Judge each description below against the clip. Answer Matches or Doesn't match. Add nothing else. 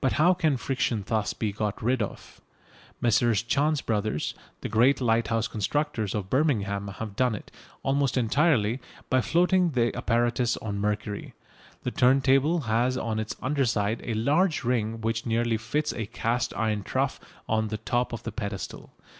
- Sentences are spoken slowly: Doesn't match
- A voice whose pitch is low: Matches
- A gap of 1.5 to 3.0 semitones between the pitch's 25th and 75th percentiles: Doesn't match